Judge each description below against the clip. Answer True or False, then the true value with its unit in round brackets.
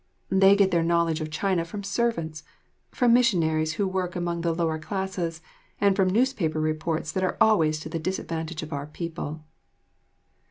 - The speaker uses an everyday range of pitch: True (3.3 semitones)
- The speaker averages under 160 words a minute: False (165 wpm)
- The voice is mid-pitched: True (170 Hz)